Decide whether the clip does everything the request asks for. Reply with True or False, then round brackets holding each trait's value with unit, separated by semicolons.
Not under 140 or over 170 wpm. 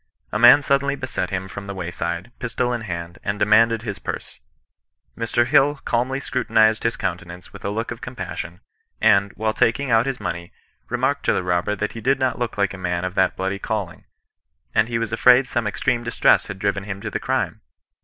False (205 wpm)